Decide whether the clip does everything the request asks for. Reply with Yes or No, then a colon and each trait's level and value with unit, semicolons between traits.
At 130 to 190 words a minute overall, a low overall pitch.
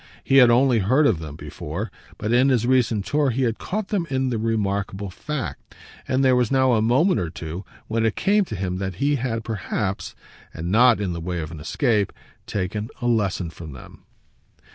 No: fast, 205 wpm; low, 115 Hz